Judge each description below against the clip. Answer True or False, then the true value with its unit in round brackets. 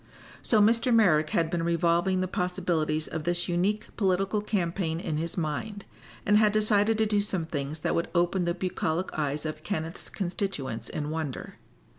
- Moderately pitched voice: True (175 Hz)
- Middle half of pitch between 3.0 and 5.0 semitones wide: True (4.1 semitones)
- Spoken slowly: False (170 wpm)